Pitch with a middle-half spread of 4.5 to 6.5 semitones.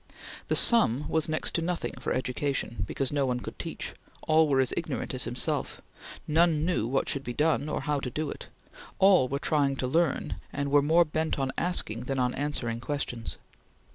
No: average, 3.6 semitones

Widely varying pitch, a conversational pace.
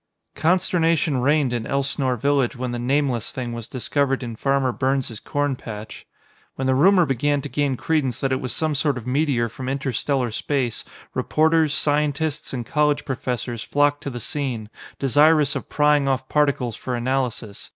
No: average, 2.8 semitones; average, 170 wpm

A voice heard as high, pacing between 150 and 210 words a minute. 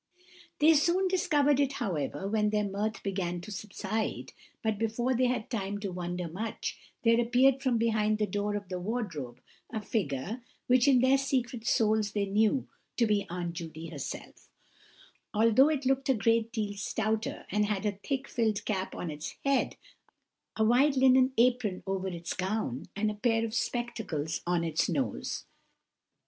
Yes: high, 215 Hz; average, 165 wpm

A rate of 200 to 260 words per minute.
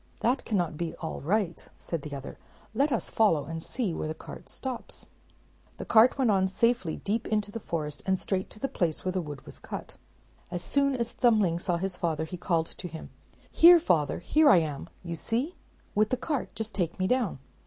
Yes: fast, 205 wpm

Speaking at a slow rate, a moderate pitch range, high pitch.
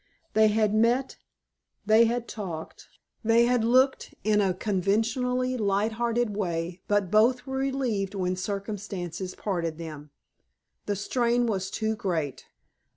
Yes: slow, 130 wpm; average, 3.9 semitones; high, 215 Hz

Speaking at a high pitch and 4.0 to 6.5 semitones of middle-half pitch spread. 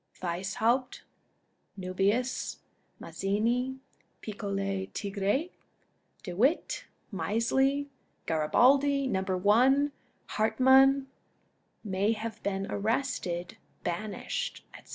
Yes: high, 215 Hz; average, 5.3 semitones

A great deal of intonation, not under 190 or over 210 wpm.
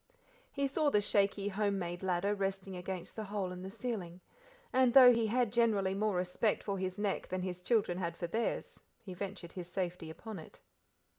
No: average, 3.0 semitones; average, 195 wpm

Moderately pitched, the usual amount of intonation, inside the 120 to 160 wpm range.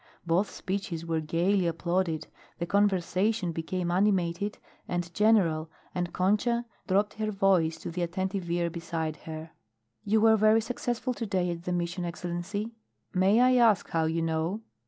Yes: medium, 180 Hz; average, 3.4 semitones; average, 155 wpm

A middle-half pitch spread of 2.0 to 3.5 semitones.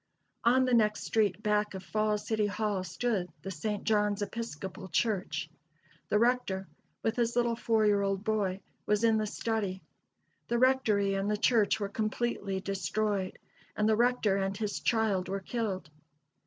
Yes: narrow, 2.4 semitones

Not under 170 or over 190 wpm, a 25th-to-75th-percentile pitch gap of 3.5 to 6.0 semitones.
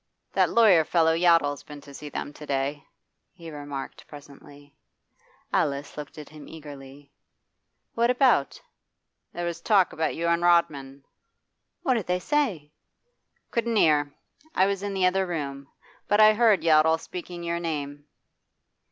No: average, 145 wpm; average, 4.1 semitones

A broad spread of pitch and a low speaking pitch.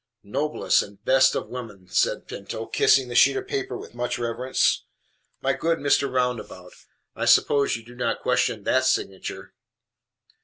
No: average, 3.1 semitones; low, 125 Hz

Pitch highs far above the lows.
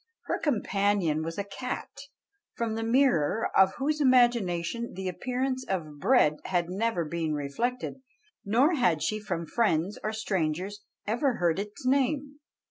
Yes: wide, 6.5 semitones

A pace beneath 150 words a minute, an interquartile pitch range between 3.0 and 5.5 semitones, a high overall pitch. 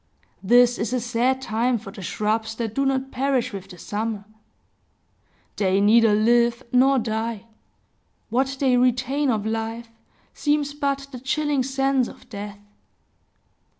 Yes: average, 140 wpm; average, 3.3 semitones; high, 240 Hz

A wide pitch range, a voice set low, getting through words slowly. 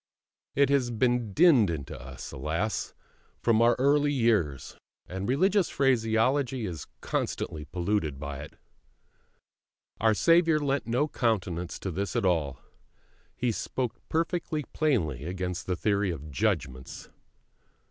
Yes: wide, 7.9 semitones; low, 110 Hz; slow, 125 wpm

